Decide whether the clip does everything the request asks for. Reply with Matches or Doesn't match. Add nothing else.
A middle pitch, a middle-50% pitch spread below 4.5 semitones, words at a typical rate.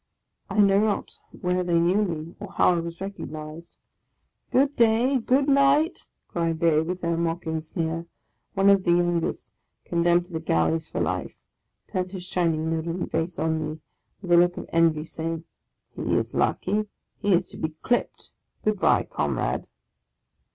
Matches